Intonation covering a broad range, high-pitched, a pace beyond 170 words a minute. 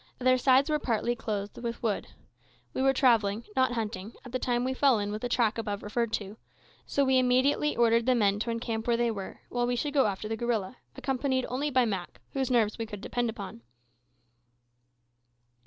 No: average, 3.1 semitones; high, 235 Hz; average, 200 wpm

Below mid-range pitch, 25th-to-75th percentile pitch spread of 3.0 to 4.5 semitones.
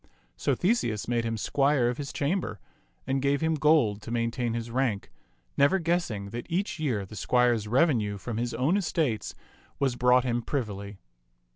Yes: low, 125 Hz; average, 4.2 semitones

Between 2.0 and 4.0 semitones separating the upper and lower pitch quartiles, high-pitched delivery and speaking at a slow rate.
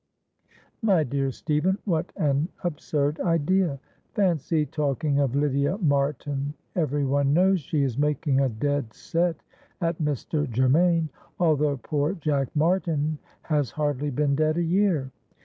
No: average, 2.9 semitones; medium, 150 Hz; slow, 130 wpm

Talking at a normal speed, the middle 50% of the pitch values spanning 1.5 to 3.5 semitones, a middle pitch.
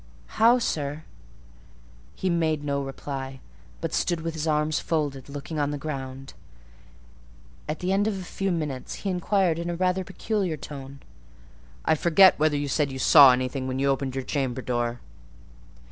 No: average, 165 wpm; average, 4.1 semitones; medium, 150 Hz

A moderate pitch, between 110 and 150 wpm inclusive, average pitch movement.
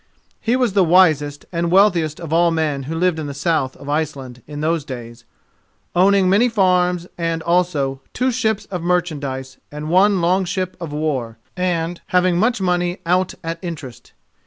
No: medium, 170 Hz; average, 175 wpm; average, 3.7 semitones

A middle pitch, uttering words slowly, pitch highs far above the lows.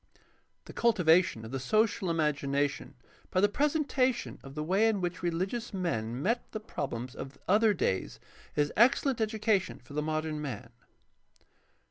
No: medium, 175 Hz; average, 145 wpm; wide, 7.4 semitones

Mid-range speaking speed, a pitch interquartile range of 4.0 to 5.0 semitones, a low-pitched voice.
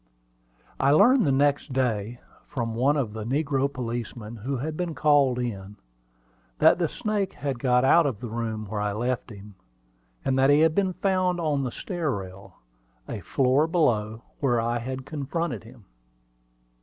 Yes: average, 170 wpm; average, 4.6 semitones; low, 130 Hz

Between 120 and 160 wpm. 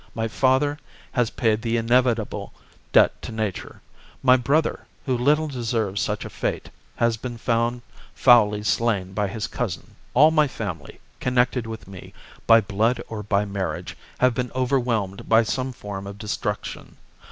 Yes: average, 150 wpm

